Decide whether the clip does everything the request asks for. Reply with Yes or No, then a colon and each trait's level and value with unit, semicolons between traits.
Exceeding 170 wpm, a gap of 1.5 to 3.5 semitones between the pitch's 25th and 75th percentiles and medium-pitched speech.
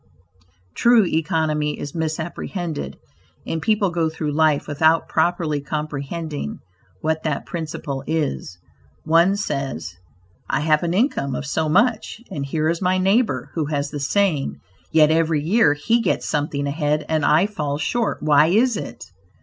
No: average, 150 wpm; average, 3.0 semitones; medium, 155 Hz